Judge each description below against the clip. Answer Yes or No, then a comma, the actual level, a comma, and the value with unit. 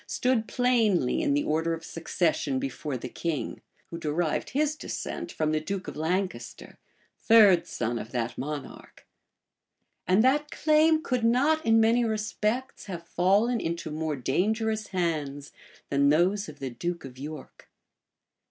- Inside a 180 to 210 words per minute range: No, average, 145 wpm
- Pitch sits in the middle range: Yes, medium, 175 Hz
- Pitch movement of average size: No, wide, 6.9 semitones